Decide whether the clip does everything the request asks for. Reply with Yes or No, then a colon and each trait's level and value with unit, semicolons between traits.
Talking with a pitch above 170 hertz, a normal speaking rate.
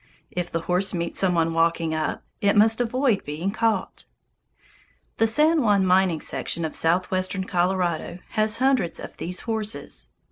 Yes: medium, 185 Hz; average, 150 wpm